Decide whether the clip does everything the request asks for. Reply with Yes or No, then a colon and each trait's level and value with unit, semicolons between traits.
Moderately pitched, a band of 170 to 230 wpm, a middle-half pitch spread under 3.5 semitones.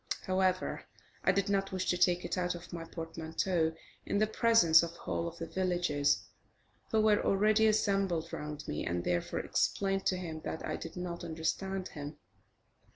Yes: medium, 180 Hz; average, 175 wpm; average, 3.0 semitones